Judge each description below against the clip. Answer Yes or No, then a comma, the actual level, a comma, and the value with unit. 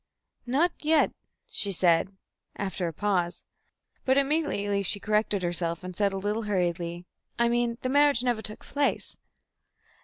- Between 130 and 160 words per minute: Yes, average, 145 wpm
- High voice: Yes, high, 205 Hz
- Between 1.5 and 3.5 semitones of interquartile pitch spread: No, wide, 5.5 semitones